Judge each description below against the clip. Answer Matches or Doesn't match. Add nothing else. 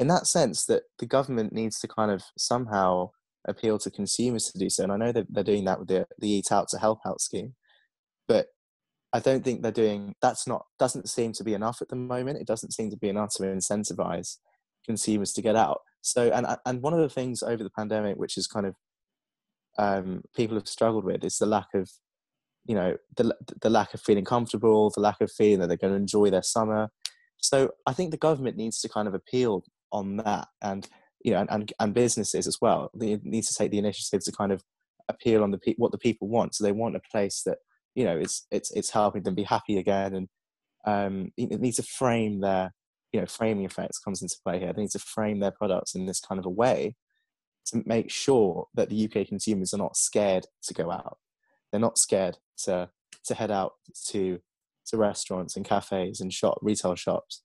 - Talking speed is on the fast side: Matches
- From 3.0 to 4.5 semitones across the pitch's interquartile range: Doesn't match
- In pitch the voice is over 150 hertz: Doesn't match